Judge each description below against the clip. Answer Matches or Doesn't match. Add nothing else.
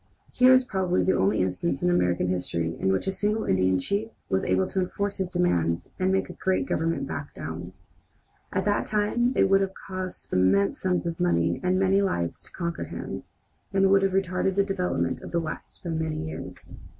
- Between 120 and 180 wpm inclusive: Doesn't match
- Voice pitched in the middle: Matches